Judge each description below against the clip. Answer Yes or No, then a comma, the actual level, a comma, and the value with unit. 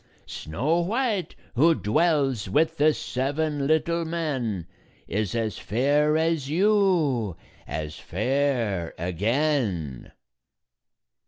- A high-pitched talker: No, medium, 140 Hz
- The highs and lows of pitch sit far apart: Yes, wide, 6.9 semitones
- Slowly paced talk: Yes, slow, 90 wpm